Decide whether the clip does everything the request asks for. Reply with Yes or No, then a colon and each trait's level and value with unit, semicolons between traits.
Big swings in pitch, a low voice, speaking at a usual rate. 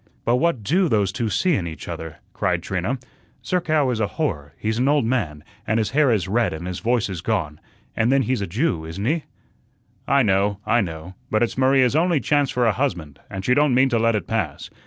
No: wide, 6.0 semitones; low, 115 Hz; fast, 225 wpm